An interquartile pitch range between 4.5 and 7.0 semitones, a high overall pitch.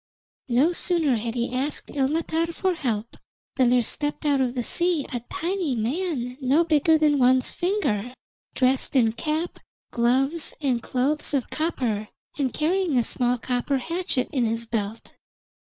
Yes: average, 4.8 semitones; very high, 270 Hz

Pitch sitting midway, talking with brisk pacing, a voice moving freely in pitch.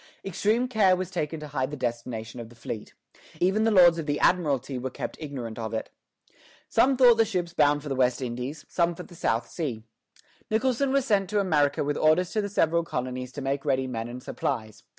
Yes: medium, 150 Hz; fast, 210 wpm; wide, 6.6 semitones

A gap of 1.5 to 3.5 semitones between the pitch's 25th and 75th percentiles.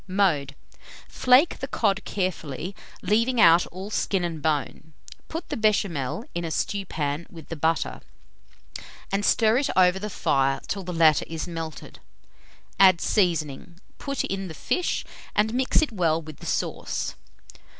No: average, 4.7 semitones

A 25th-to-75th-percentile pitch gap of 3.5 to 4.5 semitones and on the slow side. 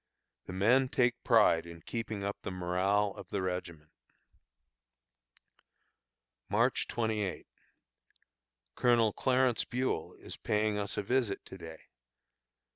Yes: average, 4.2 semitones; slow, 115 wpm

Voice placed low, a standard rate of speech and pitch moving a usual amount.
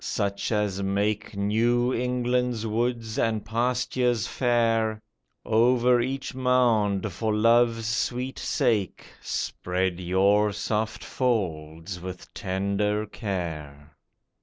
No: low, 110 Hz; slow, 95 wpm; average, 3.4 semitones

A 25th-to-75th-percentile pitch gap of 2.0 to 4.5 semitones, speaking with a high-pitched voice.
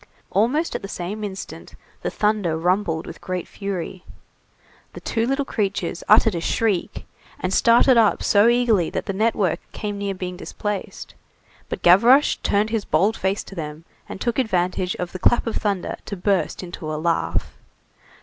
Yes: average, 3.6 semitones; high, 200 Hz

